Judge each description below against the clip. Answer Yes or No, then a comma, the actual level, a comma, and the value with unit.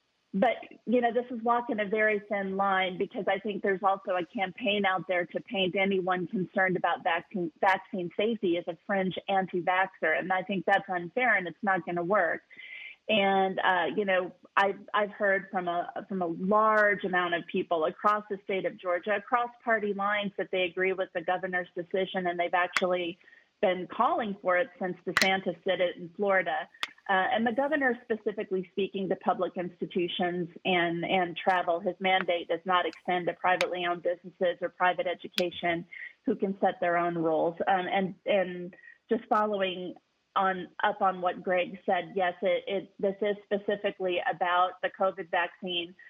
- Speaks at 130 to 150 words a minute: No, average, 175 wpm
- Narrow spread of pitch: Yes, narrow, 2.2 semitones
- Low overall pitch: No, high, 190 Hz